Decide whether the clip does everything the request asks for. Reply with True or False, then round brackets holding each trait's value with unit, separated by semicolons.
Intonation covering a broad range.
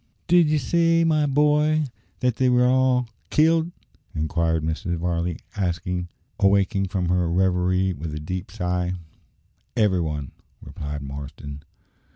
True (7.9 semitones)